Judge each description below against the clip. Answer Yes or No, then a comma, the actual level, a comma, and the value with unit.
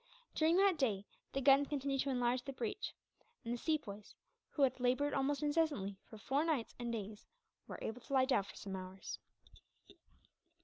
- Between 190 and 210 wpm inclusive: No, average, 175 wpm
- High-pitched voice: Yes, very high, 260 Hz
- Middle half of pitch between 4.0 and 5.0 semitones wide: Yes, average, 4.6 semitones